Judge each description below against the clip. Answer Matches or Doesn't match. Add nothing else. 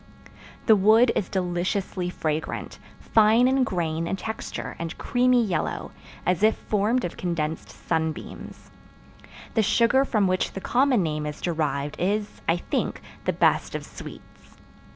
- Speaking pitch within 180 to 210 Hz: Matches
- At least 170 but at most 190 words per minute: Doesn't match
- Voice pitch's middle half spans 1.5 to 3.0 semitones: Doesn't match